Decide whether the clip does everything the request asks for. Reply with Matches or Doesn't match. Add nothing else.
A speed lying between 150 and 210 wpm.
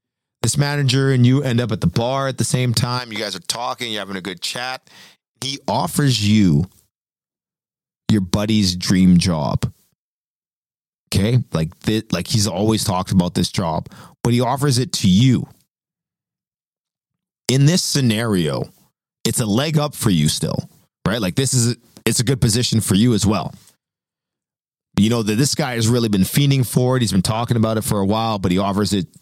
Matches